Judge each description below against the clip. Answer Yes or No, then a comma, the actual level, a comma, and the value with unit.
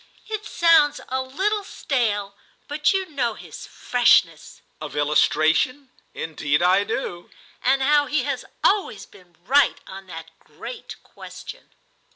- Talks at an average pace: No, slow, 130 wpm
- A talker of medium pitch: No, very high, 255 Hz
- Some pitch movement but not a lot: No, wide, 8.8 semitones